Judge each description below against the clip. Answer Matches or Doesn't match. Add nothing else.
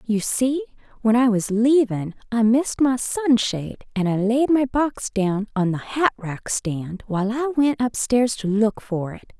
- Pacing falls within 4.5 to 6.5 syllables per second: Doesn't match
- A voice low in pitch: Doesn't match